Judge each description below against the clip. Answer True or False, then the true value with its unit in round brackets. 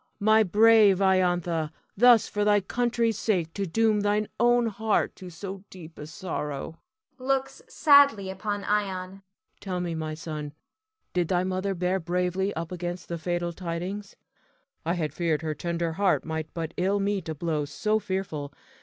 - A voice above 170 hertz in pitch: True (185 Hz)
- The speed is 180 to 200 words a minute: False (160 wpm)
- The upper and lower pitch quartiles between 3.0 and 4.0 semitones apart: True (3.7 semitones)